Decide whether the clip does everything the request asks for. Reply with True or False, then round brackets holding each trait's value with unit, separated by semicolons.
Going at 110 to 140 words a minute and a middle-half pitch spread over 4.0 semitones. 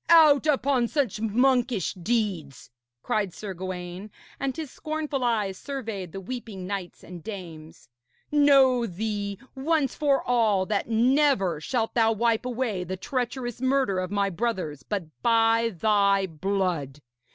True (135 wpm; 5.3 semitones)